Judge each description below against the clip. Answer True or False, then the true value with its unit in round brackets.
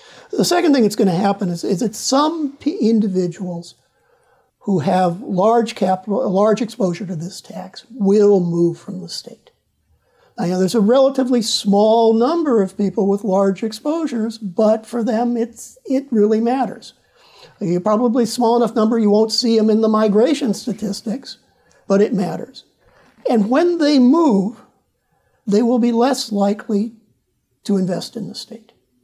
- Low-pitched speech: False (220 Hz)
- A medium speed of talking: True (160 wpm)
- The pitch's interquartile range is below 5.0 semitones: True (3.4 semitones)